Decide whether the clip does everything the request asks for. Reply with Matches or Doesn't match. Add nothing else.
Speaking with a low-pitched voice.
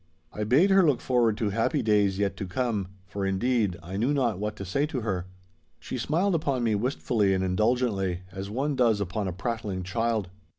Matches